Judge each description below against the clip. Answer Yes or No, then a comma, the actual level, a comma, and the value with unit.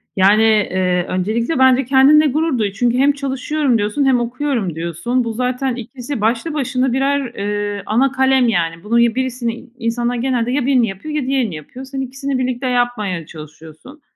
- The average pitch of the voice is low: No, high, 245 Hz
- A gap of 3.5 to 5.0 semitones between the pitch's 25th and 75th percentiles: Yes, average, 3.9 semitones